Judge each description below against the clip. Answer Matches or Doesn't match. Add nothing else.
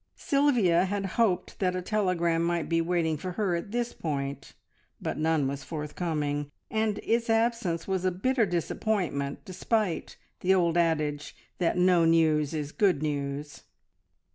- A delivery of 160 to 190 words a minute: Doesn't match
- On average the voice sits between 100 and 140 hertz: Doesn't match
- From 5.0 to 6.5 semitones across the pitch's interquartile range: Doesn't match